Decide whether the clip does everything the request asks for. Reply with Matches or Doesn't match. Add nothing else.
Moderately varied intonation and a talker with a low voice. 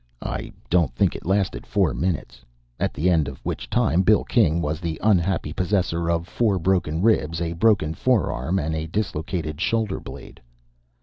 Matches